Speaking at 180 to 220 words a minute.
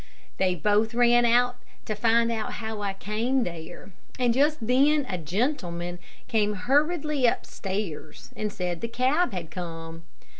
No: average, 145 wpm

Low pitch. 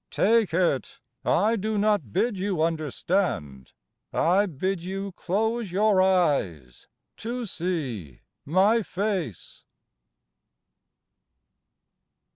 No: medium, 185 Hz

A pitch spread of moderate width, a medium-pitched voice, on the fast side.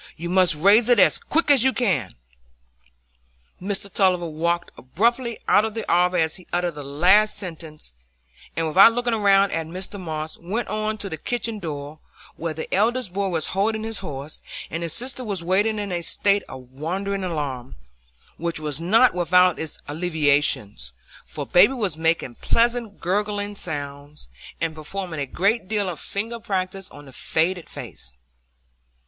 No: average, 4.6 semitones; medium, 180 Hz; average, 165 wpm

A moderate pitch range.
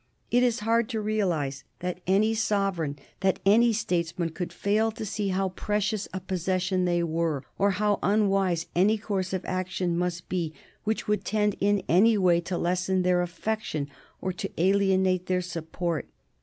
Yes: average, 3.0 semitones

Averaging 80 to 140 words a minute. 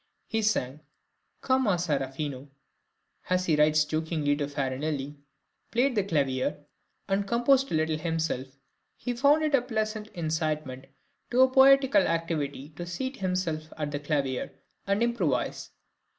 Yes: slow, 135 wpm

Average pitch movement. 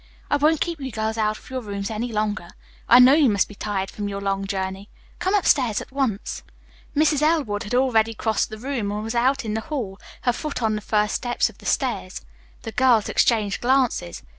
Yes: average, 4.2 semitones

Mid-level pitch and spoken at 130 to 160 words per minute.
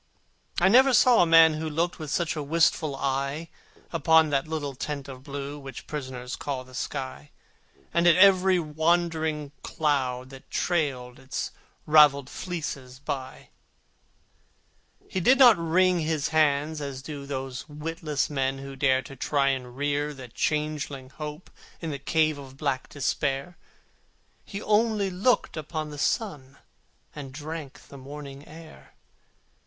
Yes: medium, 150 Hz; average, 145 wpm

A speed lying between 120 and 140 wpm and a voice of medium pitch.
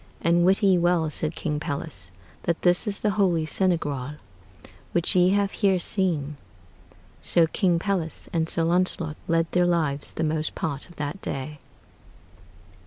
No: average, 155 wpm; medium, 170 Hz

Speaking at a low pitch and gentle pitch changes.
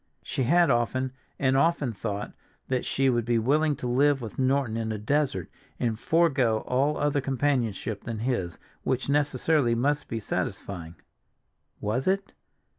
No: low, 130 Hz; average, 4.0 semitones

